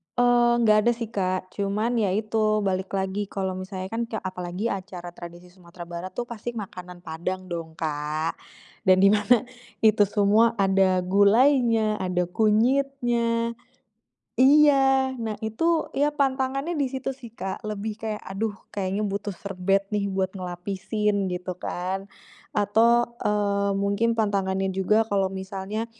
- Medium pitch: No, high, 205 Hz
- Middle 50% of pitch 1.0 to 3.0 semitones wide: No, average, 3.6 semitones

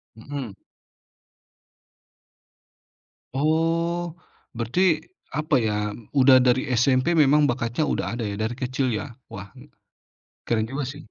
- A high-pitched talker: No, low, 130 Hz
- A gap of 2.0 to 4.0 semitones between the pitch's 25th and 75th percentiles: No, average, 4.6 semitones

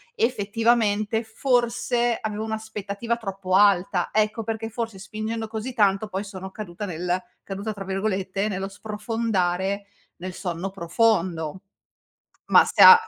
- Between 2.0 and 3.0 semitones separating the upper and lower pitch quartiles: Yes, average, 2.7 semitones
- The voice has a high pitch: Yes, high, 205 Hz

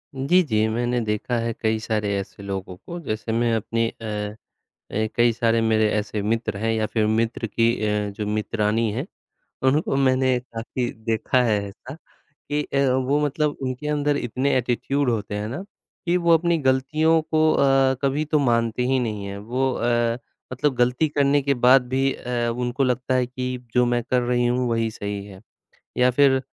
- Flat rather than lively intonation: No, average, 3.3 semitones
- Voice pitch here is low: Yes, low, 120 Hz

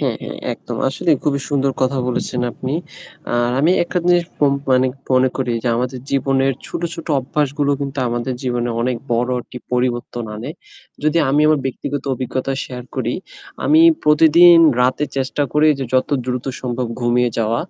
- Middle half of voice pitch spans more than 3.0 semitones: No, average, 2.7 semitones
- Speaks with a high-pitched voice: No, low, 130 Hz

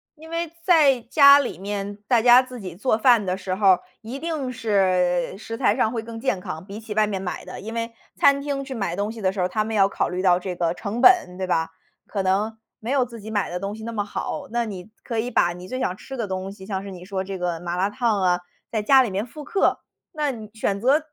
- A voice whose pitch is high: Yes, high, 210 Hz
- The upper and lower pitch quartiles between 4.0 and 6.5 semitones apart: Yes, average, 4.5 semitones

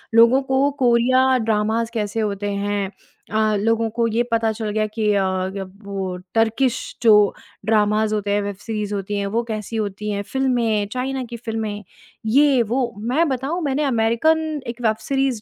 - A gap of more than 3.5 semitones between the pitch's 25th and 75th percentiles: No, average, 3.2 semitones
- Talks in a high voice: Yes, high, 225 Hz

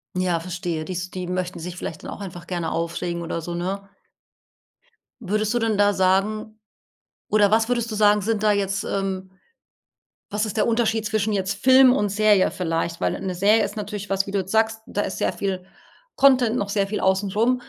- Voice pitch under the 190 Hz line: No, high, 200 Hz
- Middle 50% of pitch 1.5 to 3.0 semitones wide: Yes, average, 2.7 semitones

